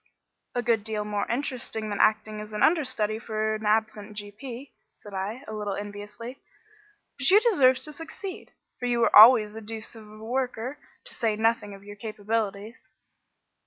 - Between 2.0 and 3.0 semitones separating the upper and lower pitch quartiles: Yes, average, 2.7 semitones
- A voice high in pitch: Yes, high, 220 Hz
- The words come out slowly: No, average, 165 wpm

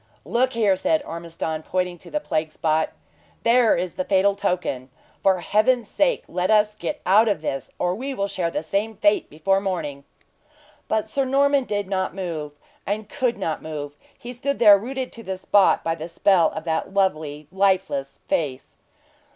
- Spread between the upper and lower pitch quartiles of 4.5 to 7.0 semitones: Yes, average, 5.2 semitones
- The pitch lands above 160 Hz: Yes, high, 190 Hz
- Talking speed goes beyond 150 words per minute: Yes, average, 175 wpm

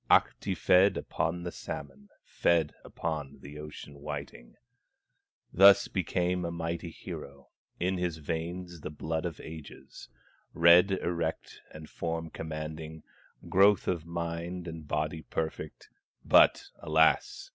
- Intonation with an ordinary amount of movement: No, narrow, 2.1 semitones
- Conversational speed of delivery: No, slow, 120 wpm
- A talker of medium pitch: No, very low, 80 Hz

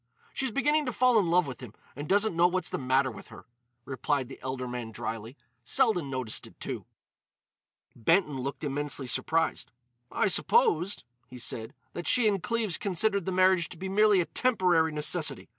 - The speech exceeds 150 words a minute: Yes, average, 175 wpm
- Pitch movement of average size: No, wide, 7.5 semitones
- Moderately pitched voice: Yes, medium, 170 Hz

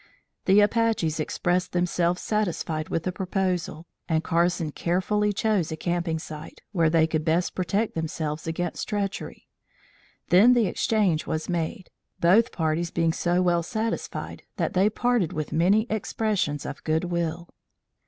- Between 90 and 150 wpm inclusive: Yes, average, 145 wpm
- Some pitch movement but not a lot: Yes, average, 3.7 semitones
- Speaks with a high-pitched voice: No, medium, 175 Hz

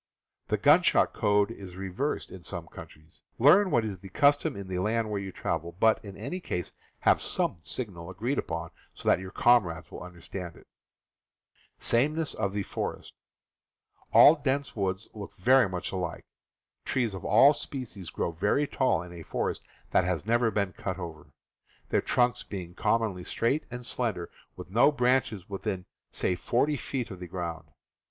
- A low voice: Yes, low, 100 Hz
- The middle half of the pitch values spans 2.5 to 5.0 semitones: No, wide, 5.4 semitones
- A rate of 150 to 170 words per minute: Yes, average, 160 wpm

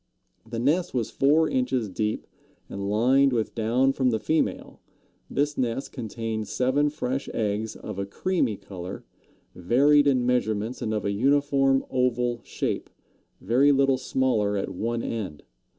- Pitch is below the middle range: Yes, low, 125 Hz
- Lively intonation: No, average, 4.0 semitones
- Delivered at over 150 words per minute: No, average, 145 wpm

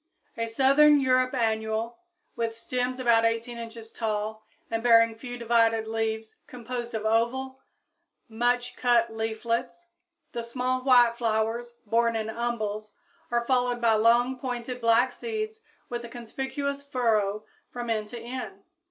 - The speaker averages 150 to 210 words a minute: No, slow, 135 wpm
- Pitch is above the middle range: Yes, high, 235 Hz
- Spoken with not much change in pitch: Yes, narrow, 1.8 semitones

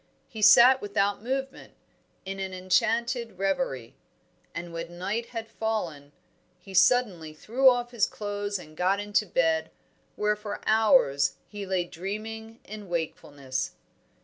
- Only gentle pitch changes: No, average, 4.3 semitones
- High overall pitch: Yes, high, 205 Hz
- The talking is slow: Yes, slow, 130 wpm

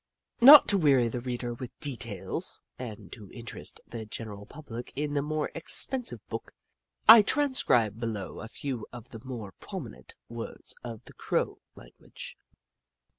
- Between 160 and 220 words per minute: No, average, 150 wpm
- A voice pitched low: Yes, low, 120 Hz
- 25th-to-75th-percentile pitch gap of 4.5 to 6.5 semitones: Yes, average, 4.8 semitones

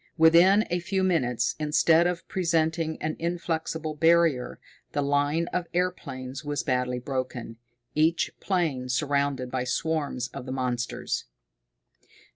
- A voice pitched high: No, medium, 155 Hz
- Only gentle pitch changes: No, average, 4.6 semitones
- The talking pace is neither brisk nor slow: No, slow, 120 wpm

